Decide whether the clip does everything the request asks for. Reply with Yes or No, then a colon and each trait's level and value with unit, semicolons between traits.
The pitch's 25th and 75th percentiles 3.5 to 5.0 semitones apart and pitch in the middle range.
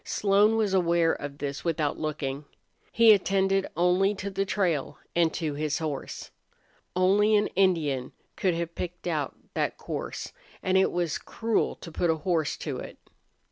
Yes: average, 3.9 semitones; medium, 175 Hz